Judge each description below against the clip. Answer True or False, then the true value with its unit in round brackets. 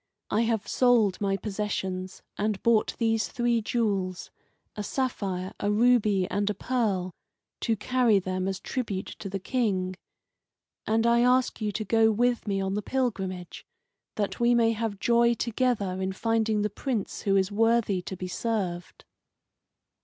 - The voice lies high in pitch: True (210 Hz)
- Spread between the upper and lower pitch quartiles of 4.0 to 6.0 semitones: False (3.4 semitones)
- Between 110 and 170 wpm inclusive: True (155 wpm)